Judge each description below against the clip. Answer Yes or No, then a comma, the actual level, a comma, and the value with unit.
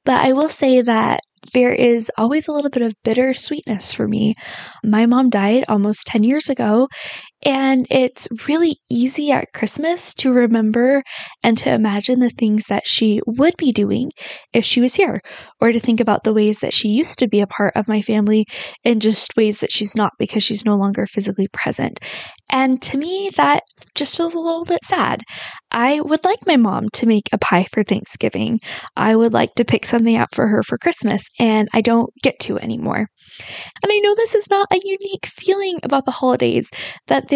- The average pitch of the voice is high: Yes, high, 245 Hz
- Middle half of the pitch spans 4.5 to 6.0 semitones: Yes, average, 4.9 semitones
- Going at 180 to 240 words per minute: Yes, average, 200 wpm